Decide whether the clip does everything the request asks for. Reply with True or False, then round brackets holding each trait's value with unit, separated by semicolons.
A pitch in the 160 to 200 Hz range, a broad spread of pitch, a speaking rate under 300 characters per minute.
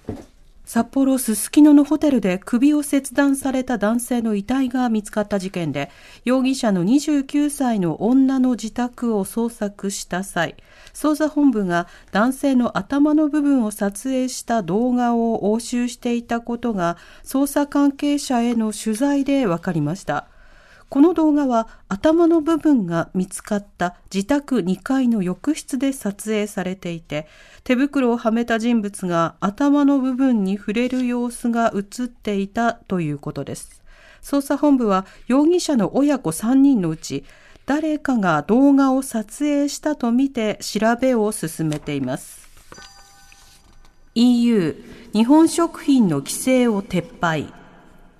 False (235 Hz; 5.7 semitones; 255 characters per minute)